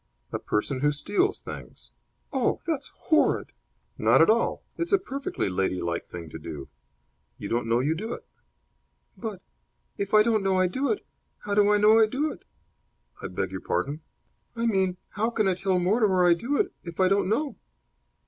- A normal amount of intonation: No, wide, 7.8 semitones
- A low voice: No, high, 195 Hz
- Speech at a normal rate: Yes, average, 185 wpm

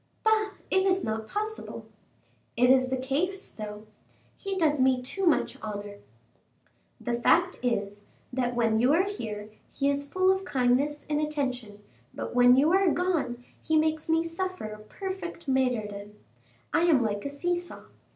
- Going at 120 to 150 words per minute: No, average, 160 wpm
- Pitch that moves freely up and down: Yes, wide, 6.8 semitones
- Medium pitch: No, very high, 280 Hz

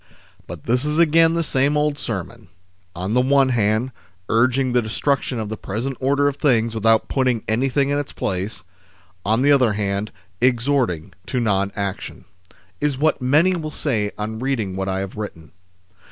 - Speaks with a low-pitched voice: Yes, low, 120 Hz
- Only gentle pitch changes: No, average, 4.9 semitones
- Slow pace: No, average, 175 wpm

